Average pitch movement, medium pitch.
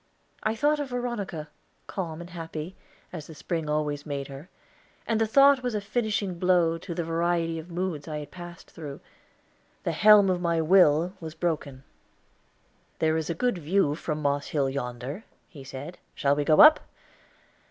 Yes: average, 4.2 semitones; medium, 165 Hz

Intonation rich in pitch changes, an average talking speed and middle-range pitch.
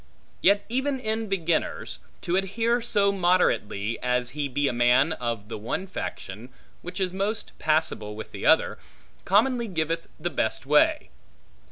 Yes: wide, 8.4 semitones; average, 145 wpm; medium, 175 Hz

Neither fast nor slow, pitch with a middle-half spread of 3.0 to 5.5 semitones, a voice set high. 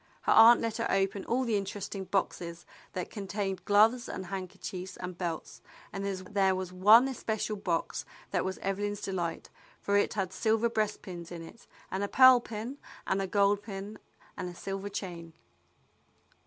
No: average, 170 wpm; narrow, 2.5 semitones; high, 195 Hz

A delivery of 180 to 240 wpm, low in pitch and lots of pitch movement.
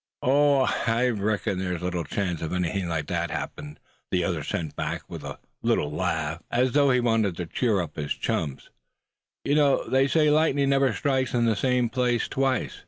Yes: average, 185 wpm; low, 115 Hz; wide, 7.1 semitones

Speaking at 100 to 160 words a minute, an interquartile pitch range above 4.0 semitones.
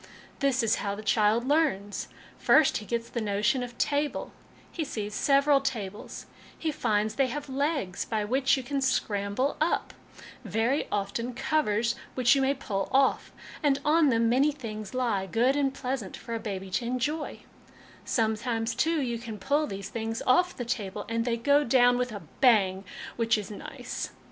No: average, 175 wpm; average, 4.4 semitones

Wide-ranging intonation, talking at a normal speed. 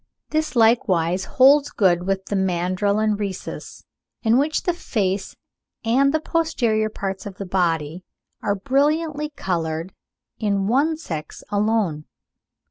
No: wide, 6.2 semitones; slow, 130 wpm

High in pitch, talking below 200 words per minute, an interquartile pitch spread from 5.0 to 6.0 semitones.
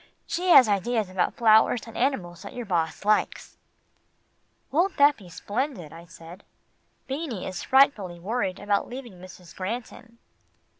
Yes: high, 210 Hz; average, 140 wpm; wide, 5.4 semitones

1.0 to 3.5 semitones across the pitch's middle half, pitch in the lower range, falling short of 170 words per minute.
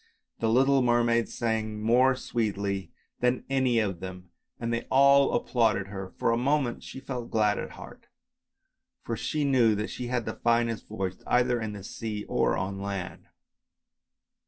Yes: average, 3.0 semitones; low, 115 Hz; average, 160 wpm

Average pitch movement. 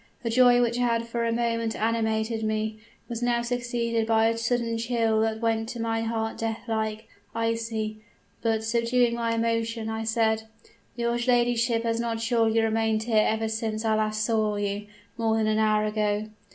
No: narrow, 1.0 semitones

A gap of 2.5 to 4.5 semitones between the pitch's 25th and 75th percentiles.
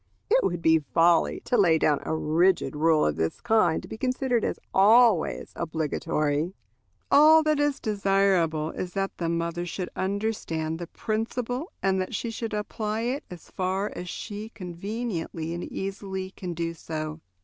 No: average, 4.9 semitones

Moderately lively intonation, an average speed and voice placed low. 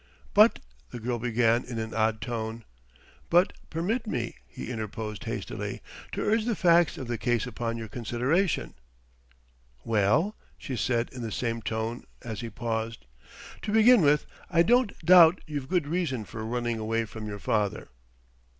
No: wide, 6.8 semitones; average, 160 wpm; low, 120 Hz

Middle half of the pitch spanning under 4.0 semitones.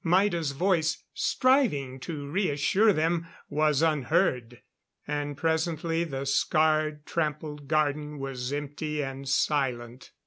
Yes: average, 2.8 semitones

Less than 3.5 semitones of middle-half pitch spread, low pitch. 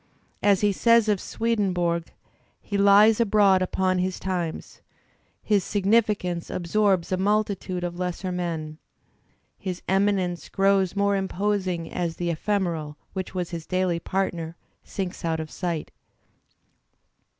No: narrow, 2.6 semitones; medium, 185 Hz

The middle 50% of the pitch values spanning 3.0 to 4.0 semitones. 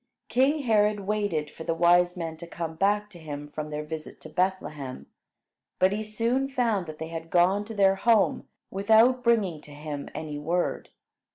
No: average, 5.1 semitones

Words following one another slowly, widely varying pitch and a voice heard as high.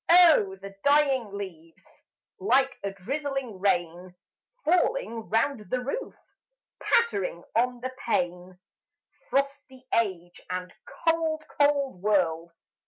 Yes: slow, 105 wpm; wide, 7.4 semitones; high, 230 Hz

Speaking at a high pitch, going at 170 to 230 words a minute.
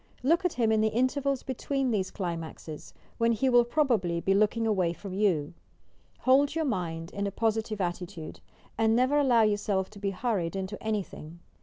Yes: high, 215 Hz; average, 190 wpm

